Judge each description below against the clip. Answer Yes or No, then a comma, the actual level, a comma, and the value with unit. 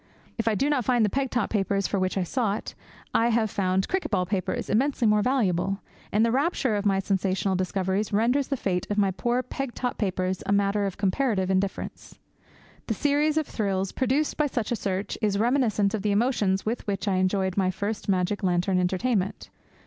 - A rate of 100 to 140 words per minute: No, average, 200 wpm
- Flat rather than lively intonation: No, average, 4.1 semitones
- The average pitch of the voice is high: Yes, high, 205 Hz